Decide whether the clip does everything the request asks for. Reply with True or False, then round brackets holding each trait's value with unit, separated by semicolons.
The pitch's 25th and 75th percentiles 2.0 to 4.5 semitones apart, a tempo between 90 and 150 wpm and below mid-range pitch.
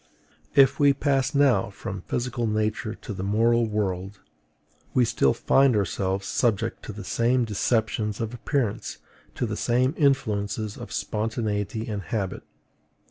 True (3.3 semitones; 135 wpm; 110 Hz)